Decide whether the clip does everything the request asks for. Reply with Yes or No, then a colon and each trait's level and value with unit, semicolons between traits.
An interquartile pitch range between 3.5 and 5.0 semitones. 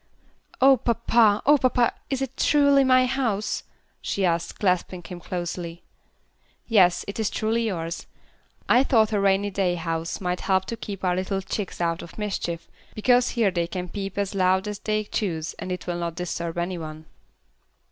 Yes: average, 4.1 semitones